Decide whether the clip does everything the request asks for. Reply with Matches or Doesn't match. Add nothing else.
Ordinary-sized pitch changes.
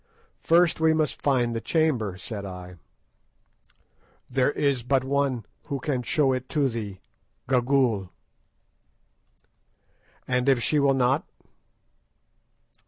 Matches